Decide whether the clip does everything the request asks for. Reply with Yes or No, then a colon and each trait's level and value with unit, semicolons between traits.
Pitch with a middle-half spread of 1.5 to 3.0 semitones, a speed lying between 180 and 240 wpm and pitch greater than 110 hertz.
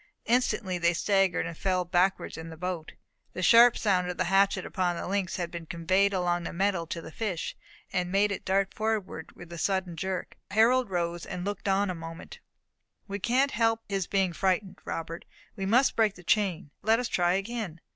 Yes: average, 2.7 semitones; average, 195 wpm; high, 190 Hz